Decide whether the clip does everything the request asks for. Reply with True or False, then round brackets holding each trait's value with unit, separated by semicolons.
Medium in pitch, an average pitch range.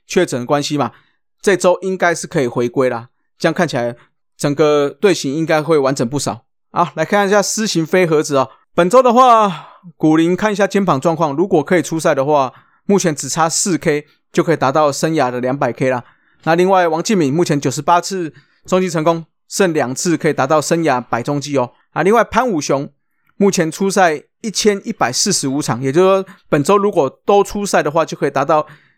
True (165 Hz; 4.4 semitones)